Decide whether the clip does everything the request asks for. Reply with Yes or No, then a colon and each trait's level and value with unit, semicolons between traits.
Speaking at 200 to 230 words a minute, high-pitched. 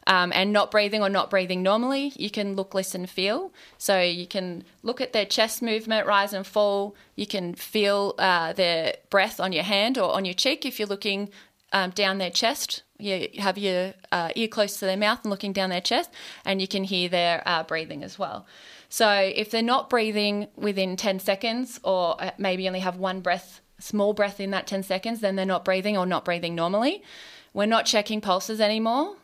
Yes: fast, 205 wpm; high, 200 Hz